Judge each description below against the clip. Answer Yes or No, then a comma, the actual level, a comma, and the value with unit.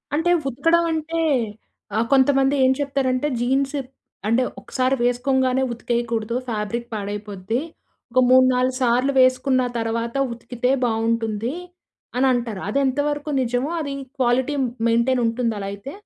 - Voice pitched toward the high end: Yes, very high, 250 Hz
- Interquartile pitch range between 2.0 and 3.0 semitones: Yes, average, 2.7 semitones